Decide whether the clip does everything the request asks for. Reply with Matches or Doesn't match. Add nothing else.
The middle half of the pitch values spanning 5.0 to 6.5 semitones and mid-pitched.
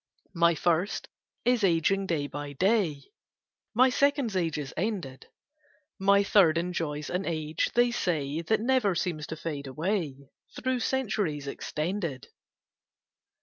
Matches